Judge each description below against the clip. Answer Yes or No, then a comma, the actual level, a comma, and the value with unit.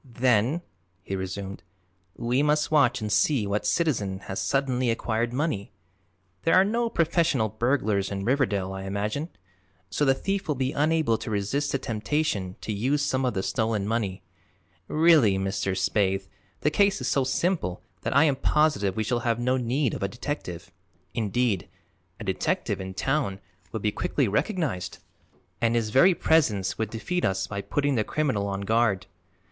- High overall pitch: No, low, 115 Hz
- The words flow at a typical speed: Yes, average, 165 wpm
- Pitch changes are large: Yes, wide, 6.2 semitones